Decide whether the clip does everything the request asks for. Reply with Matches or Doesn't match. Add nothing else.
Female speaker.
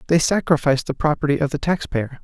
Doesn't match